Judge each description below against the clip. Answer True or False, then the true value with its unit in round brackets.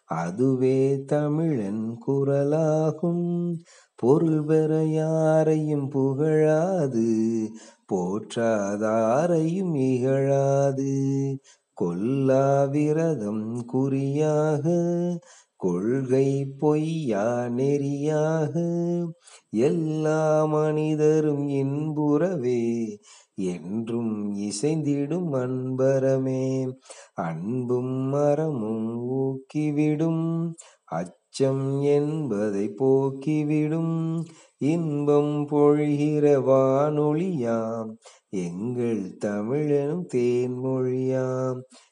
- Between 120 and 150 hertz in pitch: True (140 Hz)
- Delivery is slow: True (45 wpm)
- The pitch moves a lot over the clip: False (3.3 semitones)